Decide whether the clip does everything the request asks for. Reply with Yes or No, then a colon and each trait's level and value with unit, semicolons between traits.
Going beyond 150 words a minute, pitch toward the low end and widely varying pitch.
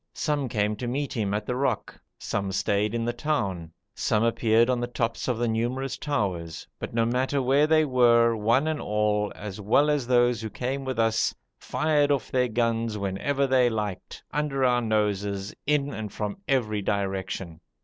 No: average, 180 wpm; low, 115 Hz; average, 4.0 semitones